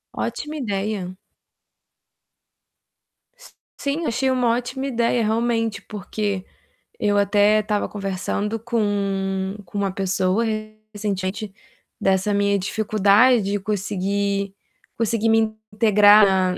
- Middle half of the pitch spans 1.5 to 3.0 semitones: Yes, narrow, 2.4 semitones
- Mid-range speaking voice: No, high, 205 Hz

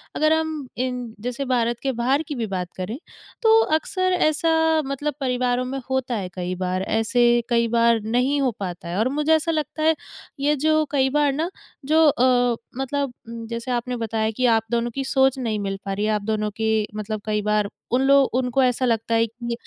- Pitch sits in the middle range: No, high, 245 Hz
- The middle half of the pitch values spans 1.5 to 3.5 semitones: No, average, 3.9 semitones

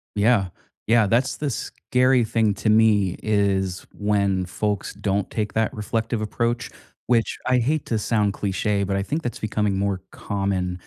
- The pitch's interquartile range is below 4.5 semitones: Yes, narrow, 2.6 semitones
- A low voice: Yes, low, 105 Hz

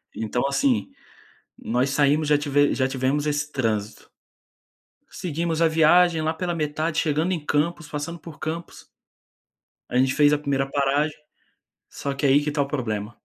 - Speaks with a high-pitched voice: No, medium, 150 Hz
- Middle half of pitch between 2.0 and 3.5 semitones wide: Yes, average, 2.7 semitones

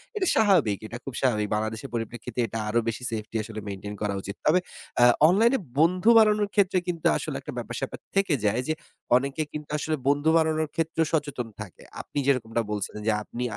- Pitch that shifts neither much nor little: No, wide, 6.8 semitones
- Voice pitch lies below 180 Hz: Yes, low, 135 Hz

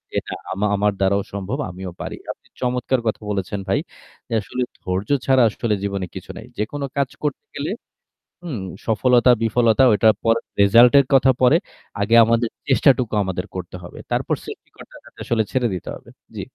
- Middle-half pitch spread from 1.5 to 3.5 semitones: No, average, 4.2 semitones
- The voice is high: No, low, 115 Hz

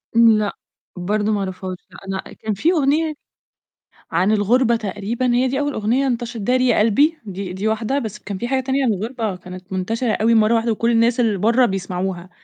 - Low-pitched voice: No, high, 220 Hz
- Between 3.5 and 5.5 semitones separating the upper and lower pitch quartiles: Yes, average, 3.9 semitones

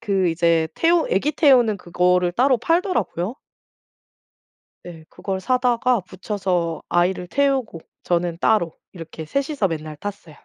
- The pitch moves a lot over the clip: Yes, wide, 6.4 semitones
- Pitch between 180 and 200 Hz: Yes, high, 190 Hz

